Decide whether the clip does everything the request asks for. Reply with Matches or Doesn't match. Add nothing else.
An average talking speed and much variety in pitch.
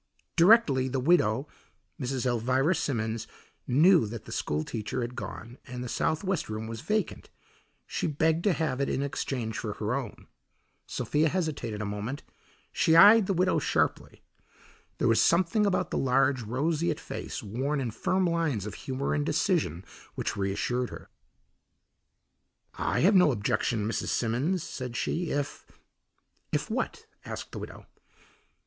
Matches